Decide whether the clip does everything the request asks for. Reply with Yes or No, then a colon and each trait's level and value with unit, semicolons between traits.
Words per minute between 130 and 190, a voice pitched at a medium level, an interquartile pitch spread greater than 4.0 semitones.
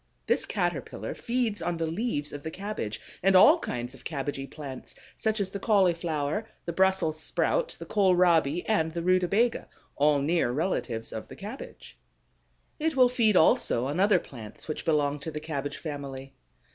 Yes: average, 165 wpm; medium, 165 Hz; wide, 5.4 semitones